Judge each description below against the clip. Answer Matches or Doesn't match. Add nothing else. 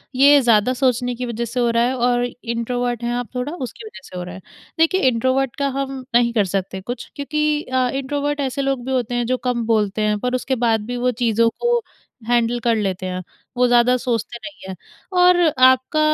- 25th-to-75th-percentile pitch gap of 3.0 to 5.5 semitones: Doesn't match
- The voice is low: Doesn't match